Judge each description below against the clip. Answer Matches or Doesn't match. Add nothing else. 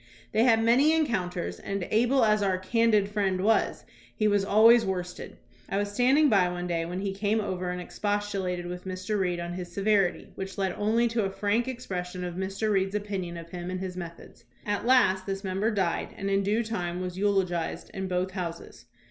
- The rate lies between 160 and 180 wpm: Doesn't match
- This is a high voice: Matches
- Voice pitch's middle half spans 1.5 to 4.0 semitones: Matches